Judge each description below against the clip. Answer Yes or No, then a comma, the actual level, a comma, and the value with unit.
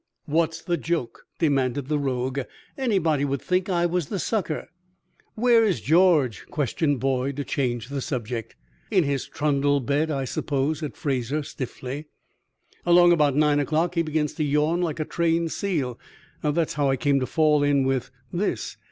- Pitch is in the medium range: Yes, medium, 150 Hz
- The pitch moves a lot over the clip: No, average, 3.6 semitones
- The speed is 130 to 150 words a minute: No, average, 165 wpm